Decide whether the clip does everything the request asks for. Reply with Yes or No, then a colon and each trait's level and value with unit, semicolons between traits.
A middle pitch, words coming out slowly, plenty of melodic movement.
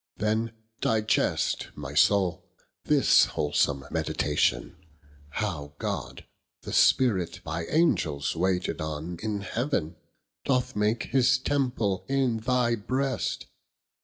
No: low, 105 Hz; slow, 105 wpm; wide, 7.4 semitones